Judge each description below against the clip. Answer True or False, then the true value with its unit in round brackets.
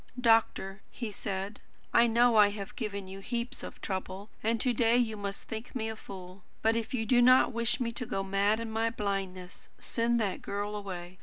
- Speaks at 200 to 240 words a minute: True (205 wpm)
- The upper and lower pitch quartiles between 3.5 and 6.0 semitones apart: False (2.9 semitones)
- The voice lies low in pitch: False (215 Hz)